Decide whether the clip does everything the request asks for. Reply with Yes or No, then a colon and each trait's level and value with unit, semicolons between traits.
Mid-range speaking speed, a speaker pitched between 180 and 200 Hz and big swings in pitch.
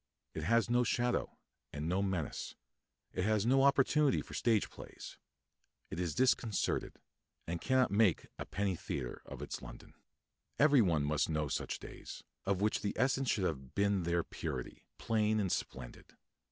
No: average, 160 wpm; low, 100 Hz; wide, 6.1 semitones